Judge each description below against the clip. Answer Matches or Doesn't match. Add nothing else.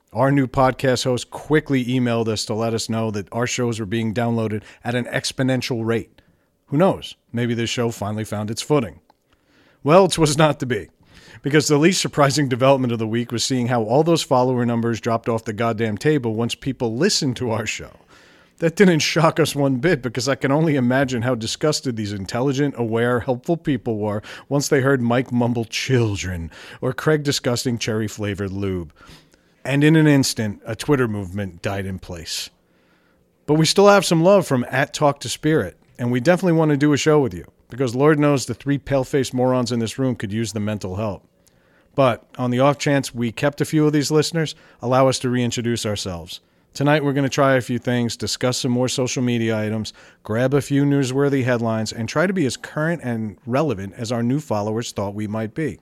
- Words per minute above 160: Matches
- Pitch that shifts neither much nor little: Matches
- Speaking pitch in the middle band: Doesn't match